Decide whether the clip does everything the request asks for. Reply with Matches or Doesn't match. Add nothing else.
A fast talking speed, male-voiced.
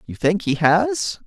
Doesn't match